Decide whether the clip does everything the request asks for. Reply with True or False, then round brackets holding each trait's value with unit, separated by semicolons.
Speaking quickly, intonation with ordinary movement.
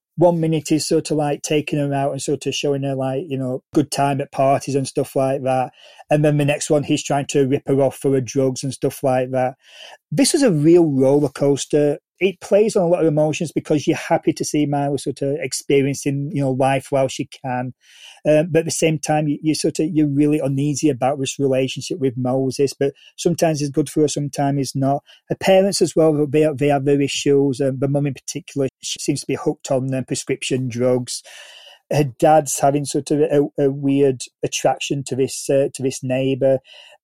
False (220 wpm; 2.1 semitones)